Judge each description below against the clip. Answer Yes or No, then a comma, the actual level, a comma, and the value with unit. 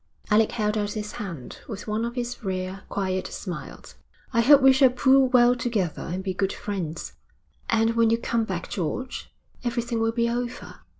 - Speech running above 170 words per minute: Yes, average, 180 wpm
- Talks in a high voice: Yes, high, 225 Hz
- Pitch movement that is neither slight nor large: Yes, average, 3.8 semitones